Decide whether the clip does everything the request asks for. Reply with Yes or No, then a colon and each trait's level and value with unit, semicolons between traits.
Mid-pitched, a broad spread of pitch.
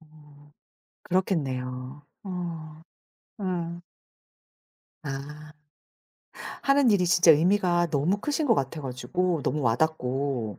No: medium, 155 Hz; average, 4.5 semitones